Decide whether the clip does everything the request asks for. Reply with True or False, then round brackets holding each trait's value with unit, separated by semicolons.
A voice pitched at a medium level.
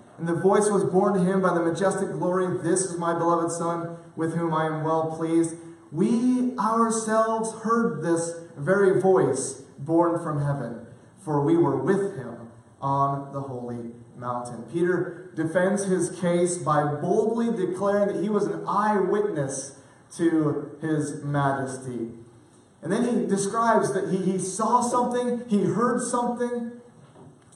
True (175 Hz)